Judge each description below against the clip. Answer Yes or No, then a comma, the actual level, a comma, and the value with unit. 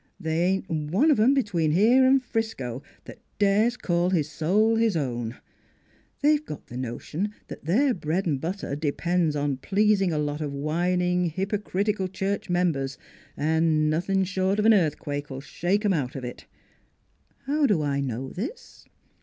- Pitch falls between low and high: Yes, medium, 175 Hz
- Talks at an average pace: Yes, average, 165 wpm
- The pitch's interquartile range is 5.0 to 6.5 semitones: Yes, wide, 5.6 semitones